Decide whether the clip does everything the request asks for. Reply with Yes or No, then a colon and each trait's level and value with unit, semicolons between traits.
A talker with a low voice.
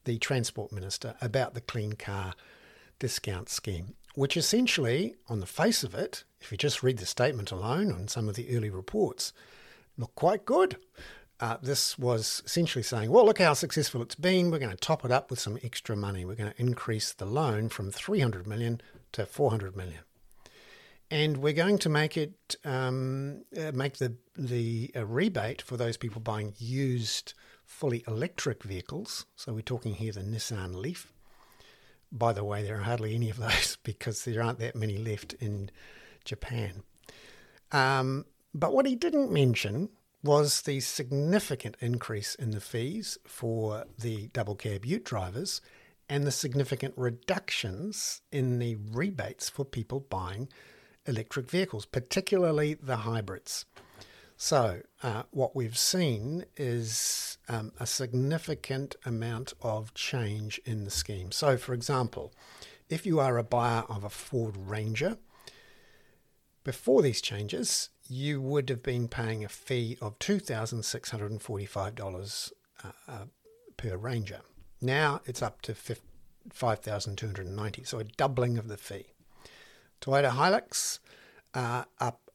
Yes: low, 120 Hz